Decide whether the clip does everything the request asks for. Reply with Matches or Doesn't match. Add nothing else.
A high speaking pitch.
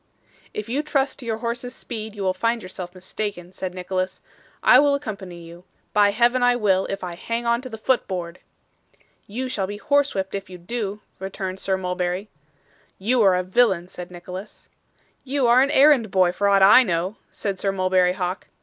Matches